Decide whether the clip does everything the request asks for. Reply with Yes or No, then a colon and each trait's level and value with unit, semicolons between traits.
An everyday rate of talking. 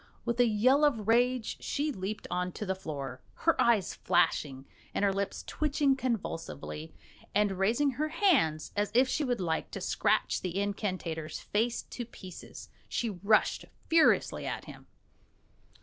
Yes: average, 150 wpm